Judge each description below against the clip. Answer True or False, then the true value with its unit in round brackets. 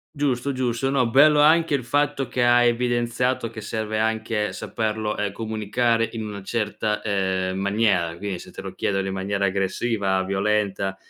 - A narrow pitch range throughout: False (3.5 semitones)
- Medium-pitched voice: False (110 Hz)